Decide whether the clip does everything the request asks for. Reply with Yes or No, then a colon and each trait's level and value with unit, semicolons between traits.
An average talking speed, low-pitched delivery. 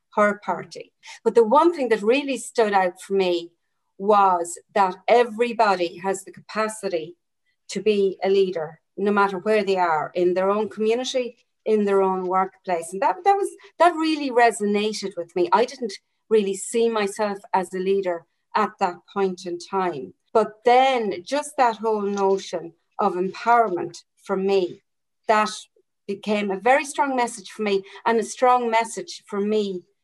No: average, 160 wpm; high, 205 Hz